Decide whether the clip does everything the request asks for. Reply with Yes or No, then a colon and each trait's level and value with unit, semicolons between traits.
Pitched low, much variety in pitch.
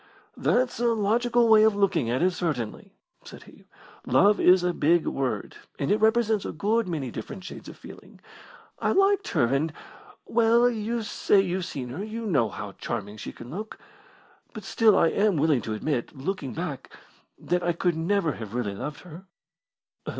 No: medium, 180 Hz; wide, 7.9 semitones